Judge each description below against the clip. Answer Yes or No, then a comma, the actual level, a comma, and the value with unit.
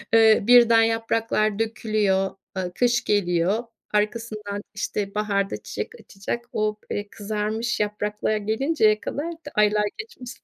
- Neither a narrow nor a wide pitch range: No, narrow, 1.7 semitones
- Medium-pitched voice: No, high, 215 Hz